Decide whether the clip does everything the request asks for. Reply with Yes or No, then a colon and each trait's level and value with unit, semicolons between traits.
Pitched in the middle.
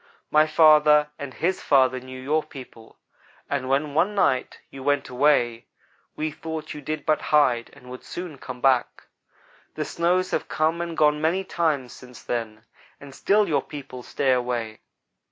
Yes: medium, 145 Hz